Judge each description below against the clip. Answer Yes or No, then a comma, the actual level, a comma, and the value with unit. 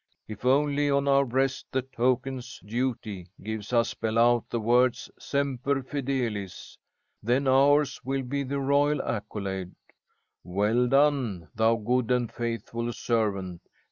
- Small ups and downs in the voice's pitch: No, average, 3.7 semitones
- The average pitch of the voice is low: Yes, low, 125 Hz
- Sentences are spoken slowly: Yes, slow, 130 wpm